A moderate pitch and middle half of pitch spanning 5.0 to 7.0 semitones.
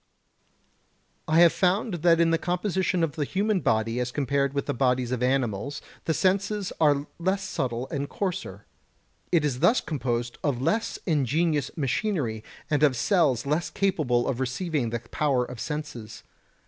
Yes: medium, 145 Hz; wide, 5.6 semitones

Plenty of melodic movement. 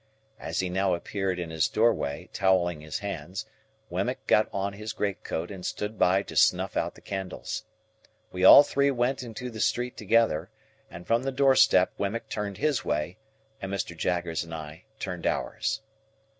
No: average, 4.1 semitones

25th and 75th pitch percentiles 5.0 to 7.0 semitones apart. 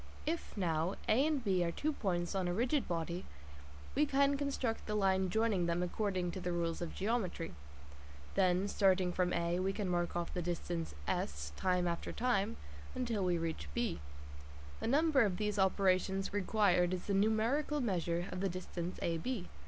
No: average, 3.9 semitones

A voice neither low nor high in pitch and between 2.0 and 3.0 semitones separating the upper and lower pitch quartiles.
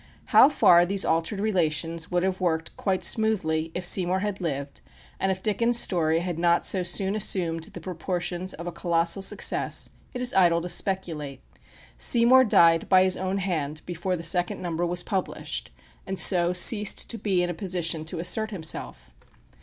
Yes: medium, 180 Hz; narrow, 2.5 semitones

